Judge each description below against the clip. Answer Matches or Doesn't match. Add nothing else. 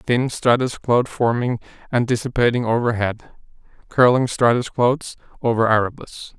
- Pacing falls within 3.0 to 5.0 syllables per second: Matches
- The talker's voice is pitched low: Matches